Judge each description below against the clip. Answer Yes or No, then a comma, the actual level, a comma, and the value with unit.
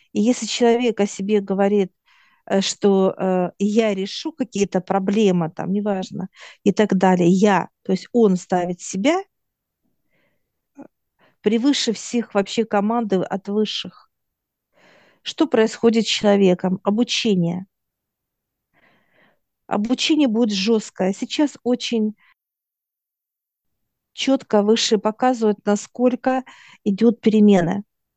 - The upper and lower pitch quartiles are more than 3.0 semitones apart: Yes, average, 3.4 semitones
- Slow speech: Yes, slow, 95 wpm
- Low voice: No, high, 210 Hz